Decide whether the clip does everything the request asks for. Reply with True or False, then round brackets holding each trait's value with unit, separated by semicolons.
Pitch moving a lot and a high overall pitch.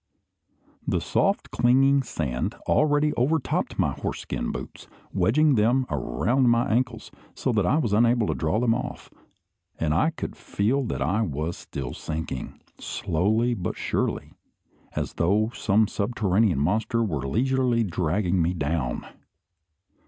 False (6.7 semitones; 110 Hz)